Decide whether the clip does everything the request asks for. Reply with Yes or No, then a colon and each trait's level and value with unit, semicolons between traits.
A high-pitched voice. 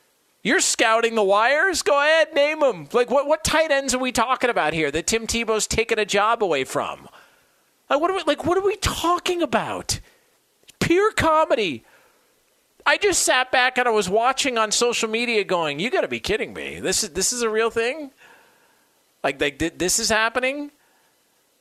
Yes: very high, 255 Hz